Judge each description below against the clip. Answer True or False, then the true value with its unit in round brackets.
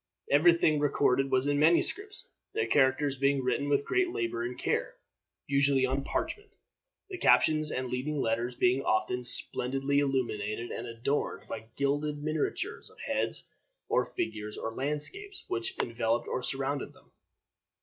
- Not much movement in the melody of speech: False (3.4 semitones)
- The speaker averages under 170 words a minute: True (145 wpm)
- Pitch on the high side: False (140 Hz)